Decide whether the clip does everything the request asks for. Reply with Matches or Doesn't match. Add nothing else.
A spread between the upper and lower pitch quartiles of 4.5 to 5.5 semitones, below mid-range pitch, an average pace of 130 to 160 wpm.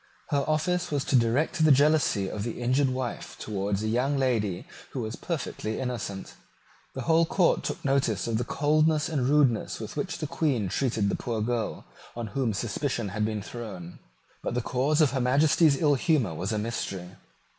Doesn't match